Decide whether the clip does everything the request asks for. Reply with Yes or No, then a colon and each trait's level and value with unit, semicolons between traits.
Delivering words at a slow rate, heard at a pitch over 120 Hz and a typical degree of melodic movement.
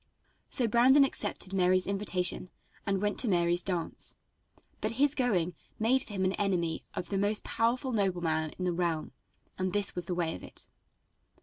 No: average, 175 wpm; high, 190 Hz; average, 3.6 semitones